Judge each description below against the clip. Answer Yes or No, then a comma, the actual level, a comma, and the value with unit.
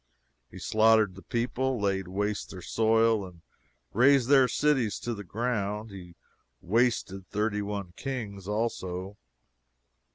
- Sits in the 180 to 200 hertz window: No, low, 105 Hz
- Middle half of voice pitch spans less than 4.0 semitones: Yes, average, 3.3 semitones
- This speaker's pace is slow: Yes, slow, 125 wpm